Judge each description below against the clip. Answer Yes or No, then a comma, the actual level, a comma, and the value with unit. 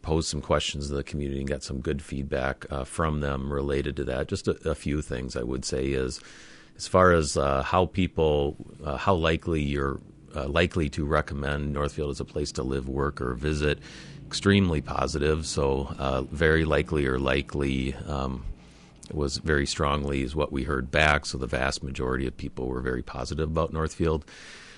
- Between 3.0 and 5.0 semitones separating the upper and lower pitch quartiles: No, narrow, 2.6 semitones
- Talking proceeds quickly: No, average, 185 wpm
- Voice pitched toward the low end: Yes, very low, 70 Hz